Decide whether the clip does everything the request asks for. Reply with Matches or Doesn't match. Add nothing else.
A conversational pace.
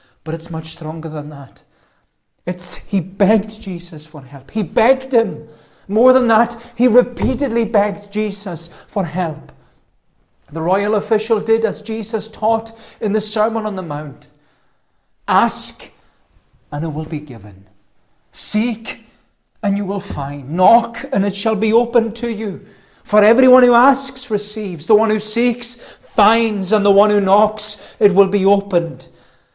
Matches